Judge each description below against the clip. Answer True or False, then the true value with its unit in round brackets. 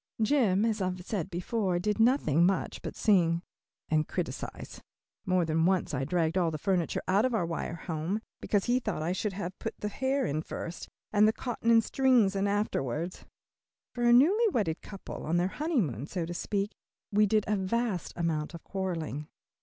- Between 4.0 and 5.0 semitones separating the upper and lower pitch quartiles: True (4.6 semitones)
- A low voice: False (190 Hz)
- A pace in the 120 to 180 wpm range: False (190 wpm)